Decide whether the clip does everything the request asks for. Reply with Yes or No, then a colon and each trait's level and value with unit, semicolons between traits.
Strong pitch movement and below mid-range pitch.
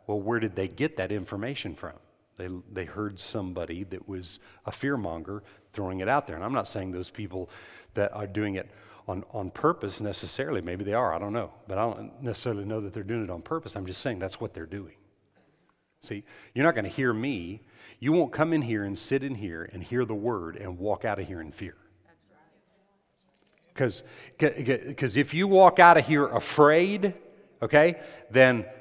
Yes: wide, 5.7 semitones; low, 105 Hz